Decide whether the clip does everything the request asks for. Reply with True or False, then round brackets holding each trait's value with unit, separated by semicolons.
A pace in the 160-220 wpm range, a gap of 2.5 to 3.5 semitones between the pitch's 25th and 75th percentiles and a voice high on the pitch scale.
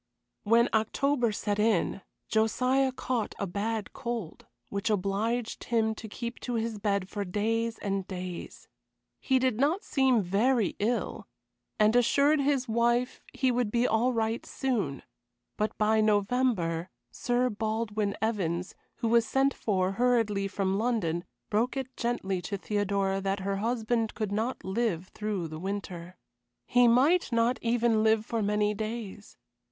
False (145 wpm; 3.2 semitones; 220 Hz)